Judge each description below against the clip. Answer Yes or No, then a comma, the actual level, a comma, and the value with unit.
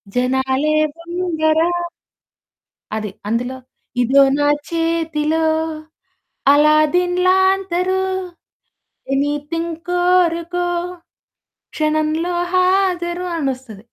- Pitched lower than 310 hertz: No, very high, 325 Hz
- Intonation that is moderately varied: Yes, average, 3.5 semitones